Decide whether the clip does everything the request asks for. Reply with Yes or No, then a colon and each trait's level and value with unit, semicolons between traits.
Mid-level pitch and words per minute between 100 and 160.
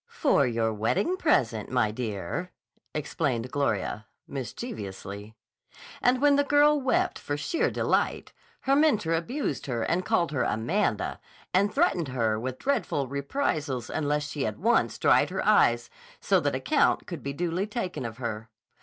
Yes: medium, 145 Hz; average, 150 wpm